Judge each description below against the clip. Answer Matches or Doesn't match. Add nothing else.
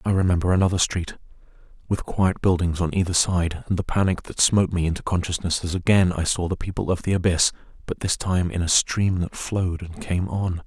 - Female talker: Doesn't match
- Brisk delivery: Matches